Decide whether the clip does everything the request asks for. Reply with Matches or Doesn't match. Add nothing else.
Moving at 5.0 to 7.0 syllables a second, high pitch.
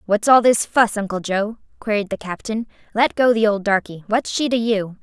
Matches